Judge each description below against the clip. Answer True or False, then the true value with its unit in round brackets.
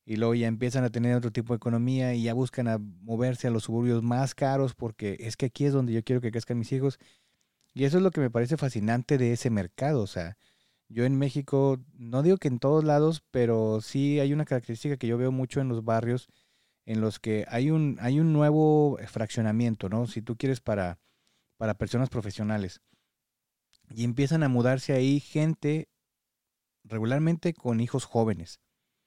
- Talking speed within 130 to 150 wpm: False (190 wpm)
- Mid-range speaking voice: False (125 Hz)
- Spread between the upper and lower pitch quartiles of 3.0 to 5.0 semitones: True (3.3 semitones)